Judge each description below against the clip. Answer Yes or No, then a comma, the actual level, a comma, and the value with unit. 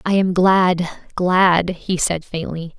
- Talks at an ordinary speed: Yes, average, 150 wpm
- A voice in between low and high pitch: Yes, medium, 180 Hz